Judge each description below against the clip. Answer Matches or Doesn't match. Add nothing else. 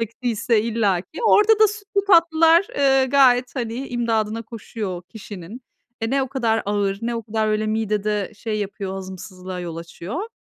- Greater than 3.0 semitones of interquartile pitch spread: Matches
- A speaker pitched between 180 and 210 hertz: Doesn't match